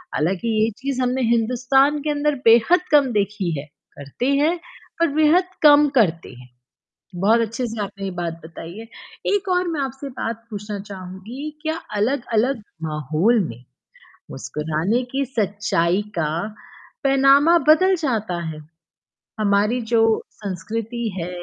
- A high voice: Yes, high, 230 Hz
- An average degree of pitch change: No, wide, 6.3 semitones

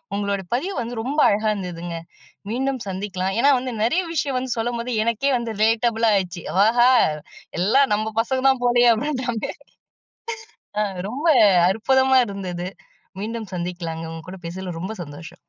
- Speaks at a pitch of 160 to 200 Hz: No, high, 225 Hz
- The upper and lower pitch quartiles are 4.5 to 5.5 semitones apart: Yes, average, 4.9 semitones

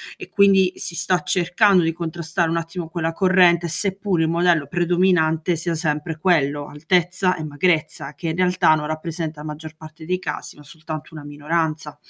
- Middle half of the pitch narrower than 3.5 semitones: Yes, narrow, 2.4 semitones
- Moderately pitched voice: Yes, medium, 165 Hz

